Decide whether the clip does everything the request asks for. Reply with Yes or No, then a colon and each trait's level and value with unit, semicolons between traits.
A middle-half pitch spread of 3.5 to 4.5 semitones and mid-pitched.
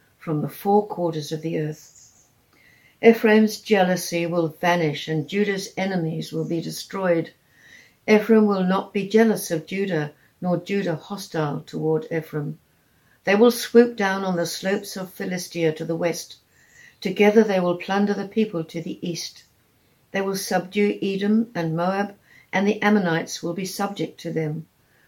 Yes: average, 3.8 semitones; medium, 180 Hz